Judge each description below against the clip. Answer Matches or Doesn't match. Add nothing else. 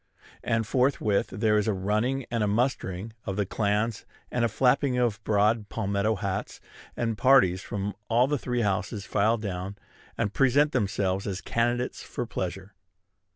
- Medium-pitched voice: Doesn't match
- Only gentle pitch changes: Doesn't match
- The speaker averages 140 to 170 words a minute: Matches